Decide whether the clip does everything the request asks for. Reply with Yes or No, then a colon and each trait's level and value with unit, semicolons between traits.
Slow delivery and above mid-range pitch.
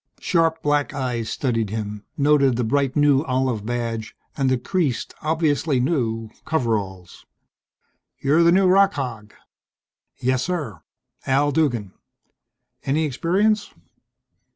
No: slow, 115 wpm; low, 135 Hz